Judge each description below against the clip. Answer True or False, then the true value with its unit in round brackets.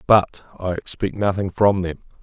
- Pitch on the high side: False (95 Hz)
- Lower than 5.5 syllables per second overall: True (4.7 syllables/s)